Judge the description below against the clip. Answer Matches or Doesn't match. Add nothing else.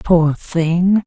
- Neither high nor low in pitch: Matches